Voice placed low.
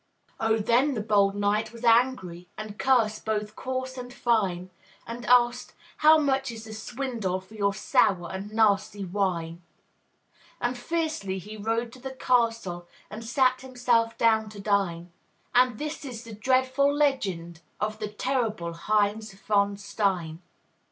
No: high, 220 Hz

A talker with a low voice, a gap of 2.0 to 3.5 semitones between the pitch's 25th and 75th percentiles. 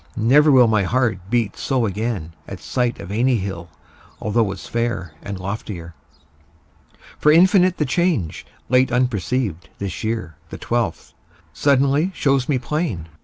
No: low, 120 Hz; average, 5.2 semitones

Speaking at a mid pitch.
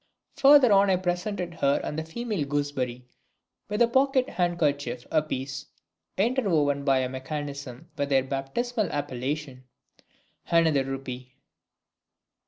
Yes: medium, 145 Hz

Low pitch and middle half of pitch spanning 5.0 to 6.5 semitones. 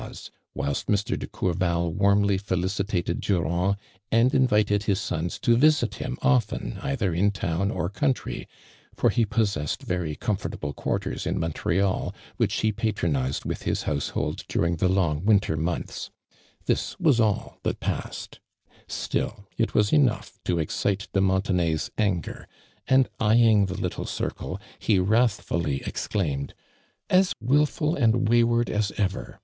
No: low, 100 Hz; average, 4.6 semitones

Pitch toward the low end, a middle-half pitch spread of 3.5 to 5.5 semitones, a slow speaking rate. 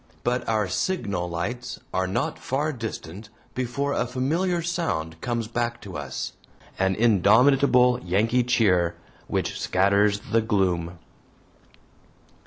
Yes: low, 110 Hz; average, 5.2 semitones; slow, 115 wpm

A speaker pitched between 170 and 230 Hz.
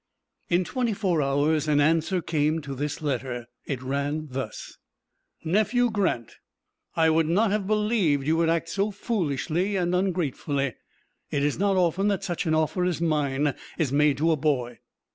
No: medium, 160 Hz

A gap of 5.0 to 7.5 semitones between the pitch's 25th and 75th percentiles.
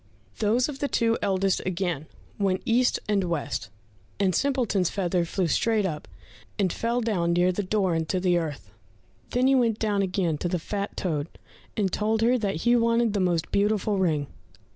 No: average, 4.3 semitones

